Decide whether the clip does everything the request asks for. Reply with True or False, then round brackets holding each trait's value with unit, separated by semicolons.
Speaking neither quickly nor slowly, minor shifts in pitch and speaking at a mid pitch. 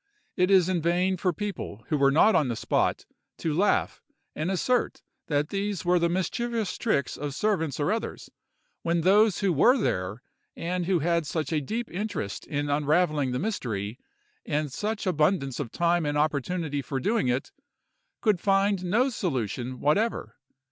False (165 wpm; 5.3 semitones; 170 Hz)